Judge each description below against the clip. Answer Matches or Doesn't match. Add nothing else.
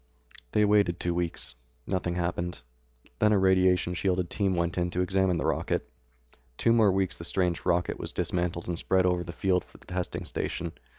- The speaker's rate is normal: Matches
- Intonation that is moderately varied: Doesn't match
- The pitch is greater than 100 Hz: Doesn't match